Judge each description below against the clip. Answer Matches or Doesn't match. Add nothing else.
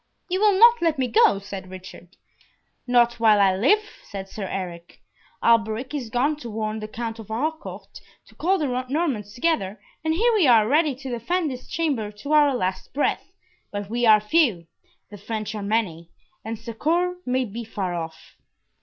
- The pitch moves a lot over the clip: Matches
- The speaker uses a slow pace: Doesn't match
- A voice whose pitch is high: Matches